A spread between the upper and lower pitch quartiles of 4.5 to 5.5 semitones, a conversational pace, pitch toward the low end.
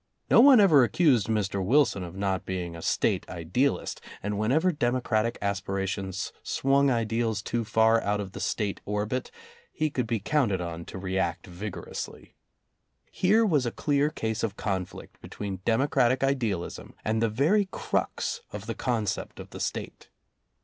Yes: average, 5.2 semitones; average, 155 wpm; low, 110 Hz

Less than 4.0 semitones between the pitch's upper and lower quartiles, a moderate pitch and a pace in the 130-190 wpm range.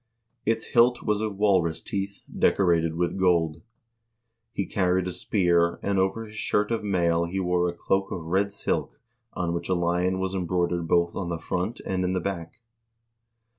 No: narrow, 2.5 semitones; very low, 90 Hz; average, 175 wpm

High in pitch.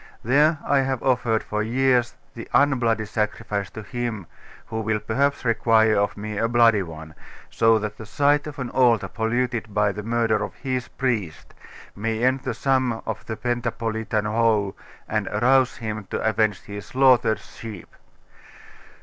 No: low, 115 Hz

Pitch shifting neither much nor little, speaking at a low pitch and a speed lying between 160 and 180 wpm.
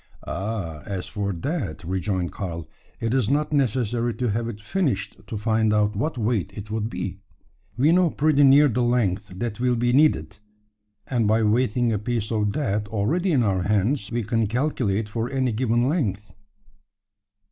Yes: average, 3.7 semitones; low, 115 Hz; average, 170 wpm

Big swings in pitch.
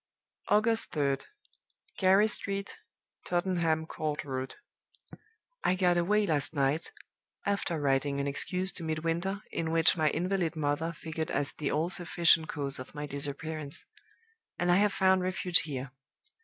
No: average, 4.0 semitones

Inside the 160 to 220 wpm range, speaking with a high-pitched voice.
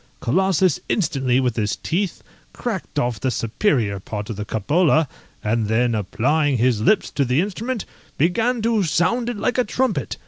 No: average, 165 wpm; medium, 145 Hz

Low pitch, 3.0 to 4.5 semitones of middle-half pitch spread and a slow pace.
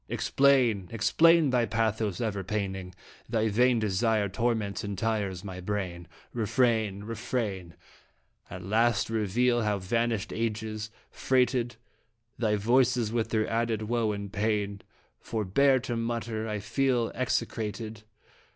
No: low, 110 Hz; narrow, 2.6 semitones; slow, 120 wpm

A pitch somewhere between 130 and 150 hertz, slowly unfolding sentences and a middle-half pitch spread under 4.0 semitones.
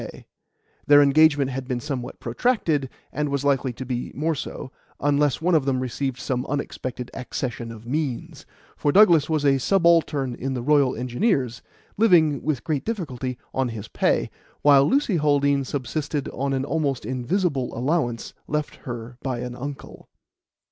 No: medium, 140 Hz; average, 155 wpm; average, 3.2 semitones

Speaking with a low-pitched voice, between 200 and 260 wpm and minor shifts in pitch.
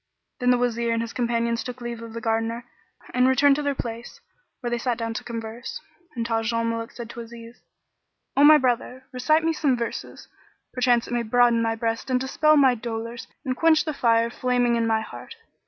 No: high, 235 Hz; fast, 205 wpm; narrow, 1.7 semitones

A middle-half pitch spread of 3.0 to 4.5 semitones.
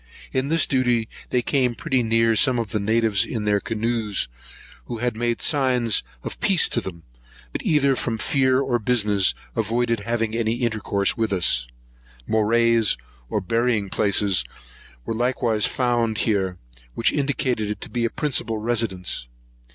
No: narrow, 2.6 semitones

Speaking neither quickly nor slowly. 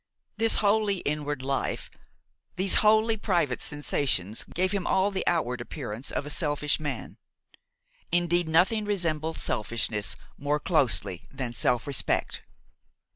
No: slow, 125 wpm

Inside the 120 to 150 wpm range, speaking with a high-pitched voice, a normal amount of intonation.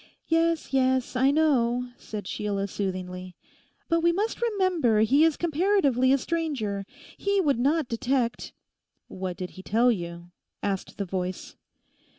No: average, 140 wpm; very high, 250 Hz; wide, 8.2 semitones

